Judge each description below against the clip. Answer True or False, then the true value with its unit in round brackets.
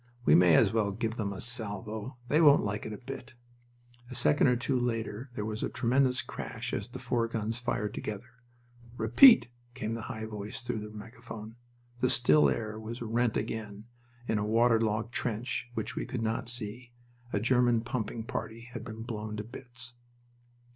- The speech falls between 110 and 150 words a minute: False (180 wpm)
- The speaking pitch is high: False (115 Hz)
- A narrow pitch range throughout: True (2.3 semitones)